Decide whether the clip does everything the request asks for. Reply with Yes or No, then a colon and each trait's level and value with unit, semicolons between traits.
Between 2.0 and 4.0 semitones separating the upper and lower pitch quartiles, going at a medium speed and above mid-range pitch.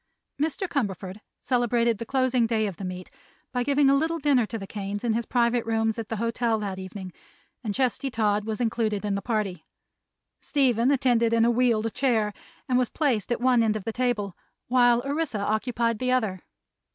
Yes: average, 3.0 semitones; average, 190 wpm; high, 230 Hz